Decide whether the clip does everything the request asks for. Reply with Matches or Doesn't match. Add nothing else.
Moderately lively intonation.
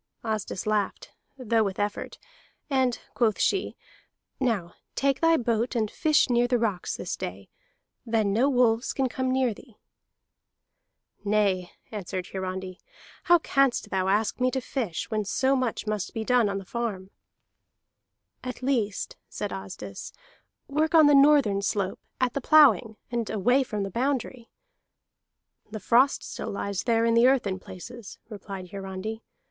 Matches